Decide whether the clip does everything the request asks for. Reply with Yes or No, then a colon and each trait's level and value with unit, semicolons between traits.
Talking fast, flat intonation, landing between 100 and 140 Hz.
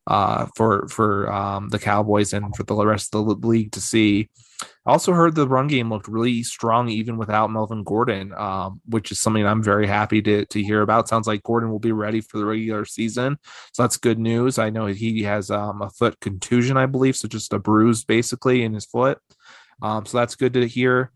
Yes: fast, 220 wpm; narrow, 2.1 semitones; low, 110 Hz